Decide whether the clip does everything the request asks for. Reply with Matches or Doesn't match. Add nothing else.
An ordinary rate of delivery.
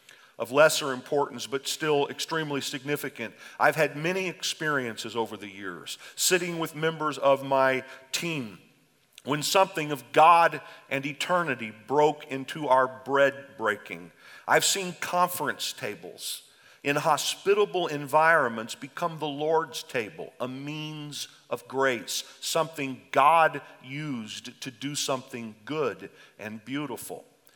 Doesn't match